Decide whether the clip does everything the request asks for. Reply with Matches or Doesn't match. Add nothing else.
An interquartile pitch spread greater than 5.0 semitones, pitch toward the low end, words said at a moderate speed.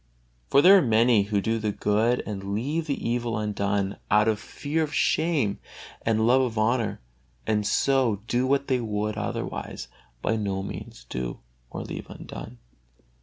Doesn't match